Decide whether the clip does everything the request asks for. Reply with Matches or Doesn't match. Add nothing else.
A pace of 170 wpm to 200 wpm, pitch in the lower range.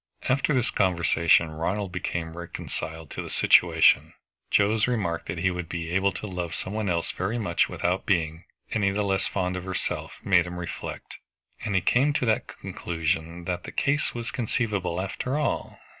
Matches